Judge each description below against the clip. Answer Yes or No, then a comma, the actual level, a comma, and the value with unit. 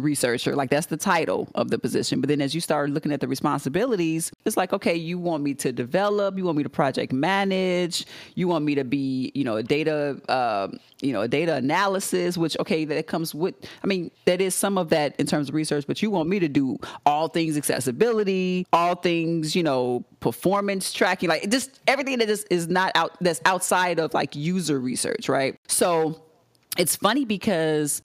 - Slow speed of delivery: No, fast, 205 wpm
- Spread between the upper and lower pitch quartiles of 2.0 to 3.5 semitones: No, average, 4.0 semitones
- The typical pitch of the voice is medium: Yes, medium, 170 Hz